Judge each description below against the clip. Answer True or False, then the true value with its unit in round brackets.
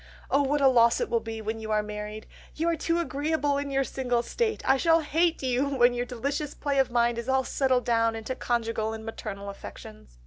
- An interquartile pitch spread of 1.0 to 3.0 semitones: False (3.9 semitones)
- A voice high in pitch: True (245 Hz)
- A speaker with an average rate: False (220 wpm)